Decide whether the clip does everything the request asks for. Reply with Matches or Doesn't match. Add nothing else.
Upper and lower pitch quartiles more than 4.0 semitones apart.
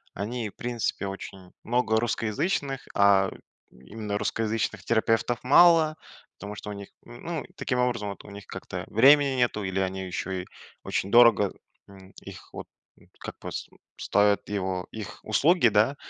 Doesn't match